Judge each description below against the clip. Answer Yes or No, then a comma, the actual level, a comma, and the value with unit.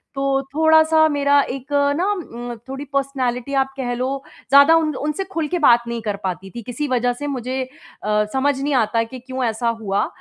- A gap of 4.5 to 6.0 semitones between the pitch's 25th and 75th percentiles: No, average, 3.3 semitones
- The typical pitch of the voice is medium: No, very high, 265 Hz